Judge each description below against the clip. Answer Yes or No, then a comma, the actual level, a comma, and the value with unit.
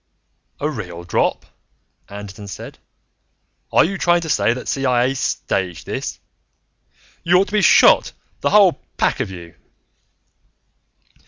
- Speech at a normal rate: No, slow, 130 wpm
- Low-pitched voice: Yes, low, 130 Hz